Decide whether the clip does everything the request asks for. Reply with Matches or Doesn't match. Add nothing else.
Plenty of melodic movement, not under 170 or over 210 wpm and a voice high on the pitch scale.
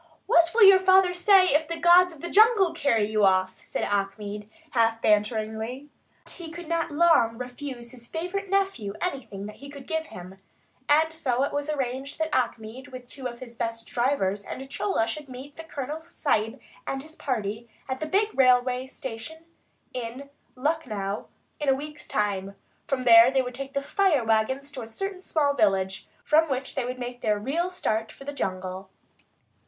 Matches